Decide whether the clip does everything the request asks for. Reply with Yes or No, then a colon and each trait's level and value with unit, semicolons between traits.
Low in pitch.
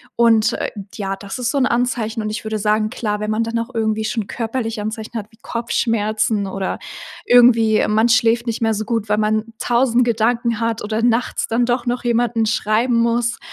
No: high, 225 Hz